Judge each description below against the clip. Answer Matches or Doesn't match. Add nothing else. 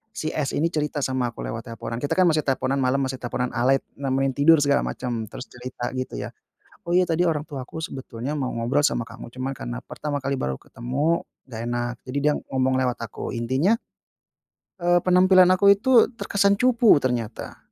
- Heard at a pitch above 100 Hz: Matches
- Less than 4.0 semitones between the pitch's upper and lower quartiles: Doesn't match